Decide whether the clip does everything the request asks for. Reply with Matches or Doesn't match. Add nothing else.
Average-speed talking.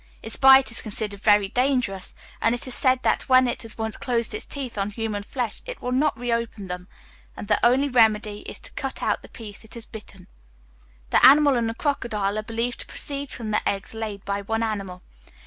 Doesn't match